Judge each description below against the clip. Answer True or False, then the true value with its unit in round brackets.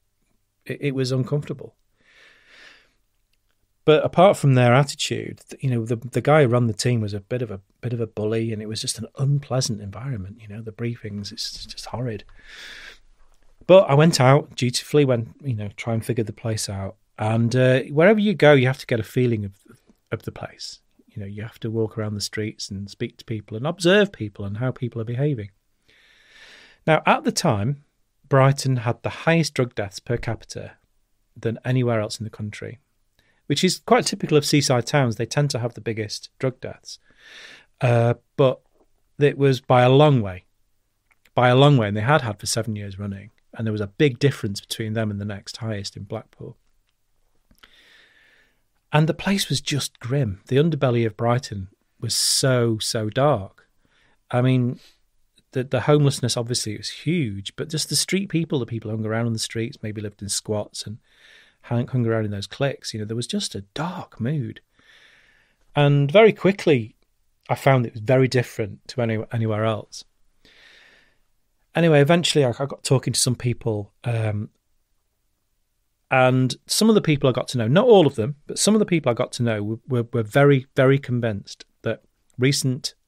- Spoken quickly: False (190 wpm)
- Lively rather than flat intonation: False (4.5 semitones)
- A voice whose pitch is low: True (120 Hz)